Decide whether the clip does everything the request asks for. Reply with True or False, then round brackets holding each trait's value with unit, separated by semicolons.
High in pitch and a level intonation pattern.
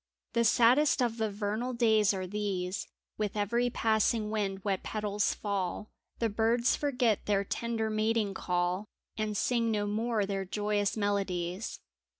True (210 Hz; 2.3 semitones)